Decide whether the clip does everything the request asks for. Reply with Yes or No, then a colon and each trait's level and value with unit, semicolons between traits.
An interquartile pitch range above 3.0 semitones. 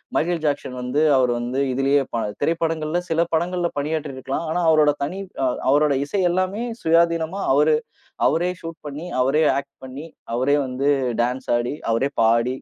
Yes: average, 3.9 semitones